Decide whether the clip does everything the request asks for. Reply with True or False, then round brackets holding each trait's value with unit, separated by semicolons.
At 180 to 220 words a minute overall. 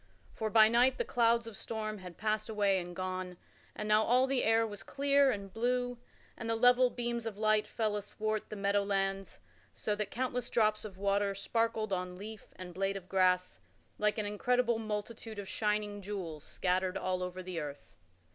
True (185 wpm)